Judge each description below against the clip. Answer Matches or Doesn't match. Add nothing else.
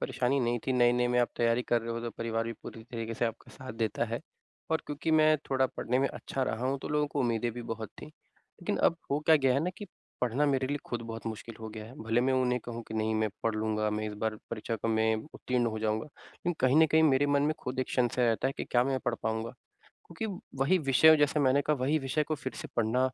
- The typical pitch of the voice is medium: Doesn't match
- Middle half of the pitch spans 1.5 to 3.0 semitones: Doesn't match